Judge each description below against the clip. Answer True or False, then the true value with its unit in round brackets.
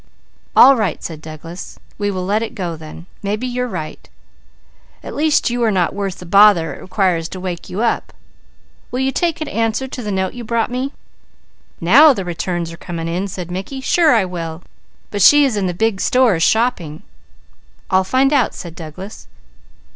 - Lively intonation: True (5.7 semitones)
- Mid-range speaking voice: False (195 Hz)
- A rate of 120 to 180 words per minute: False (190 wpm)